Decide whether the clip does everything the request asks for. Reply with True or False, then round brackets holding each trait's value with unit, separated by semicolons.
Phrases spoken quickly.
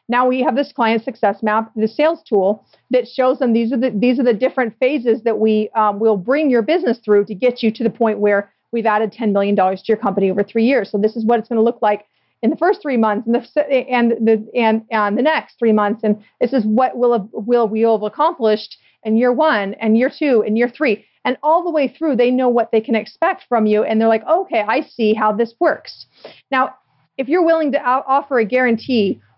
True (250 wpm)